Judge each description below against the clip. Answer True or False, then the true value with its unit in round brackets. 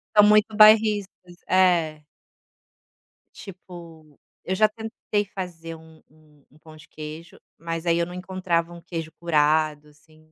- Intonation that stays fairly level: False (3.2 semitones)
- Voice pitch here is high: False (170 Hz)